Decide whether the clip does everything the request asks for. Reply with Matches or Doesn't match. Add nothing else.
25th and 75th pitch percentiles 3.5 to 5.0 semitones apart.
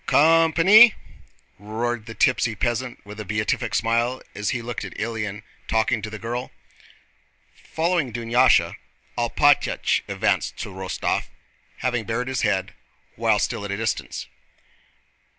Doesn't match